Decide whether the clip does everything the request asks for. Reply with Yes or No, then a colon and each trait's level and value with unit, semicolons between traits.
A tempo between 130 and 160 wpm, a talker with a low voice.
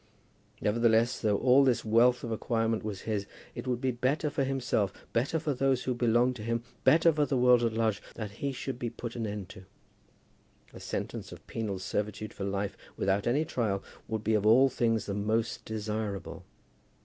No: average, 190 wpm; low, 115 Hz